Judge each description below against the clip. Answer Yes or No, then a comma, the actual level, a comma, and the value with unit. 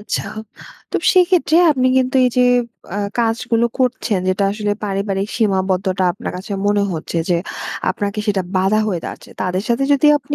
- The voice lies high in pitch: Yes, high, 205 Hz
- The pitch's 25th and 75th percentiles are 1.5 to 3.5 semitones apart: No, average, 4.5 semitones